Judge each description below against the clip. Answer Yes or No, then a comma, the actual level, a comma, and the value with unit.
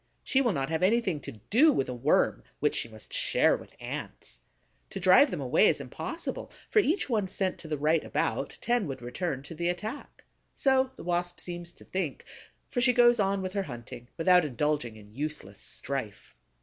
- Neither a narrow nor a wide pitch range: No, wide, 7.5 semitones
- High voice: No, medium, 175 Hz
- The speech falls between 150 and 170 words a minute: No, average, 195 wpm